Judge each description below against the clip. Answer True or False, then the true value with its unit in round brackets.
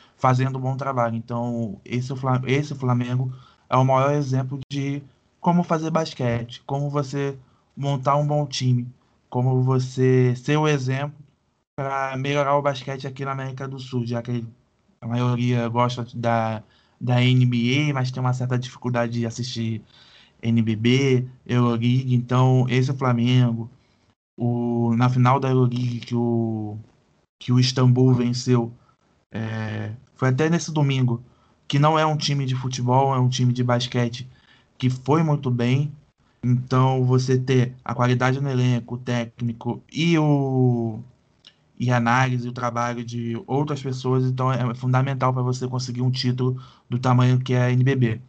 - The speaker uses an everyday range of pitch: False (1.8 semitones)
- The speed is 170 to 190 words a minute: False (150 wpm)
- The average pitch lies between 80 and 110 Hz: False (125 Hz)